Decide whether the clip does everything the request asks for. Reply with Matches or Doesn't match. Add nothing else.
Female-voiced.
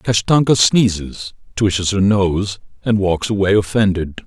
Doesn't match